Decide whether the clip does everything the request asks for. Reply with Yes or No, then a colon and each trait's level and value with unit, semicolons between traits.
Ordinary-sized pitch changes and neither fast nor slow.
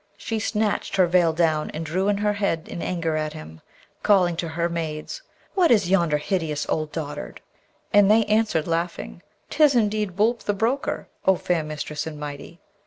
Yes: average, 4.9 semitones; average, 175 wpm